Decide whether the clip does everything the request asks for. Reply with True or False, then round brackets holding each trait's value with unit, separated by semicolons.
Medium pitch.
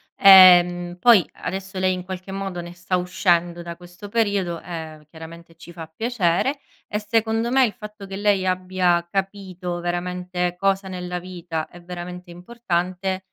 True (180 Hz)